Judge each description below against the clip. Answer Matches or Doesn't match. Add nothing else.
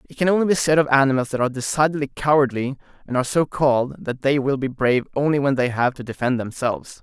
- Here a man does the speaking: Matches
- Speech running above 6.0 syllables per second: Matches